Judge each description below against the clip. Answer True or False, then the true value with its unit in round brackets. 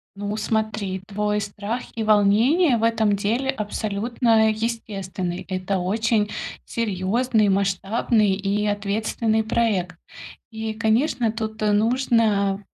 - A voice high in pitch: True (215 Hz)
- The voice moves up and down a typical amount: False (2.1 semitones)